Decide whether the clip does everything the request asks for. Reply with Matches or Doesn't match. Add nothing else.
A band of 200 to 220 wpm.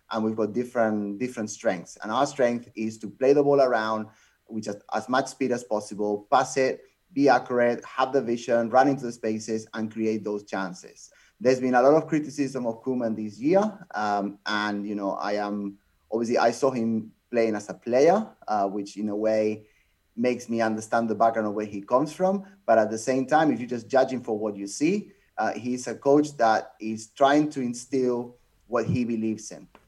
Matches